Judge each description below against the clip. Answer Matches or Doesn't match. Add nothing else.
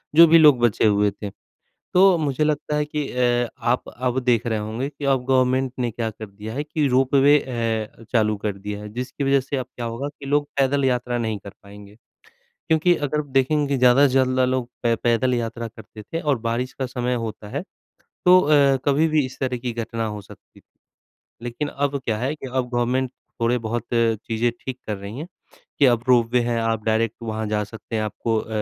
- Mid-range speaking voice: Doesn't match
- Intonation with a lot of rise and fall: Doesn't match